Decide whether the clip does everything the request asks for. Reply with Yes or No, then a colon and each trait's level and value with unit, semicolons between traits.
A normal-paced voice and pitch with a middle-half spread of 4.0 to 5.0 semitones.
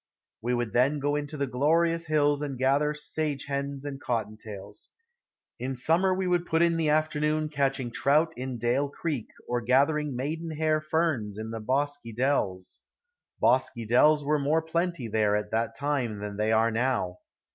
Yes: average, 175 wpm; average, 4.3 semitones